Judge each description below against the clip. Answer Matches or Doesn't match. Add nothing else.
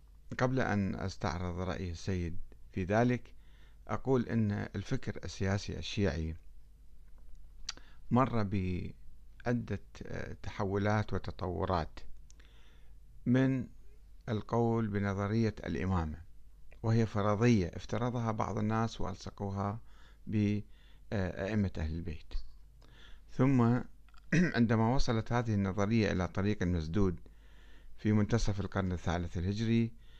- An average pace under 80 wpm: Doesn't match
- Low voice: Matches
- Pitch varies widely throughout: Doesn't match